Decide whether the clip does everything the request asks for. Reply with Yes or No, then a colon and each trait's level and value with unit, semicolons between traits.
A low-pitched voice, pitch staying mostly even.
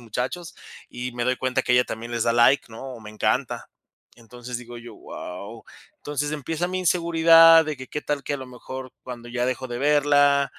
No: low, 130 Hz; average, 3.5 semitones